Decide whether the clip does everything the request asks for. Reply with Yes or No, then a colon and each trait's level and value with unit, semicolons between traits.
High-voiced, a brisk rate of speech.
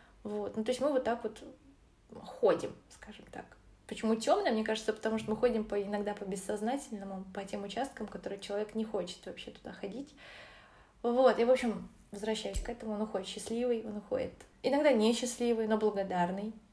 Yes: high, 220 Hz; fast, 170 wpm